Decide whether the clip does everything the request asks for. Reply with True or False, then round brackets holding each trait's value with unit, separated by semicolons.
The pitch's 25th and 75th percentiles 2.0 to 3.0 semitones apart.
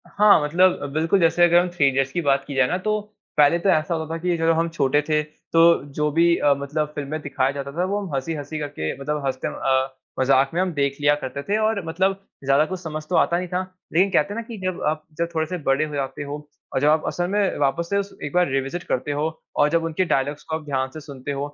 False (3.8 semitones)